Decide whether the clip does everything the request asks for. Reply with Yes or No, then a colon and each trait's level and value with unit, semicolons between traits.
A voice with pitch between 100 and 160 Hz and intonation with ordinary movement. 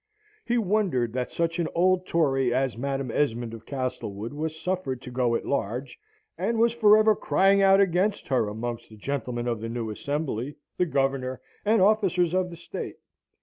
No: medium, 140 Hz; wide, 7.2 semitones